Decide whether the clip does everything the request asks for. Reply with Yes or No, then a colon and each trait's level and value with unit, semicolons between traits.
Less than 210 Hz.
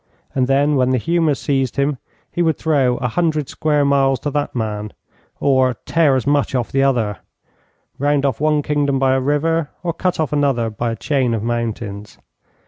Yes: low, 135 Hz